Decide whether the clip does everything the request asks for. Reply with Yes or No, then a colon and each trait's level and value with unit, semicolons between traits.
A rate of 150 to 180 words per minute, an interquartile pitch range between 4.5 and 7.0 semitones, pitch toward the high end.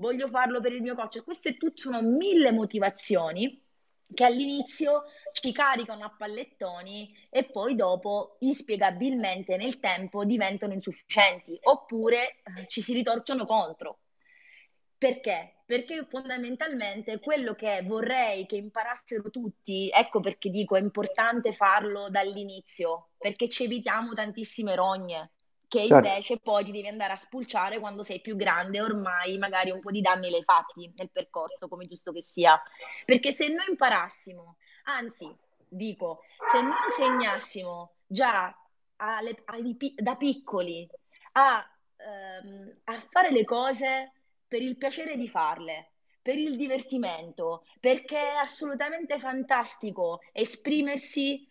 No: average, 130 wpm; wide, 5.4 semitones; high, 220 Hz